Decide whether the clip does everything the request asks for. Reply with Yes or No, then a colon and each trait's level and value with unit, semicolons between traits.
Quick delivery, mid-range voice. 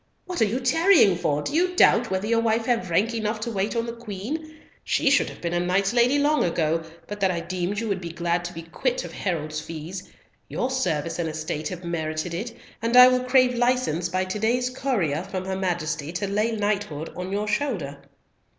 No: fast, 215 wpm; high, 200 Hz